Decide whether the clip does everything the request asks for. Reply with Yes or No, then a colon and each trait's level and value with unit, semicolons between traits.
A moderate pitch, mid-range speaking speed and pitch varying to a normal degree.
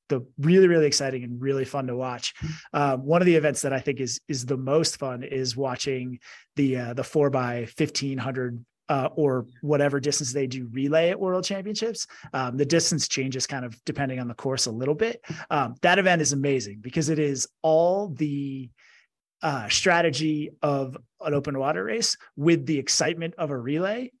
Yes: medium, 145 Hz; average, 190 wpm; average, 3.3 semitones